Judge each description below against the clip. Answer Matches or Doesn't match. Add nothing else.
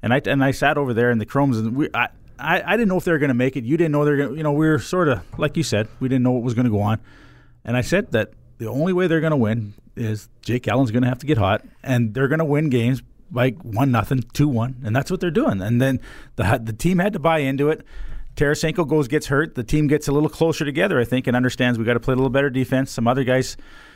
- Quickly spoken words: Matches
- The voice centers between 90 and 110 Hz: Doesn't match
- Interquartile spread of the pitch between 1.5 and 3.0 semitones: Doesn't match